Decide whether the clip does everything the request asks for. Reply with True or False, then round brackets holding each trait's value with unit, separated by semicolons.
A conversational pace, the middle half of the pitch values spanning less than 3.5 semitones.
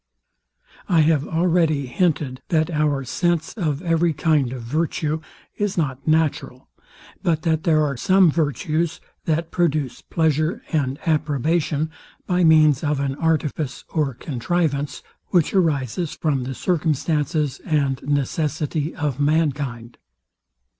False (120 wpm; 2.6 semitones)